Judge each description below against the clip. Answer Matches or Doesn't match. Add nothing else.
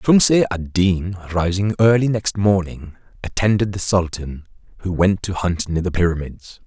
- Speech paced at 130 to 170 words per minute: Matches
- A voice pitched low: Matches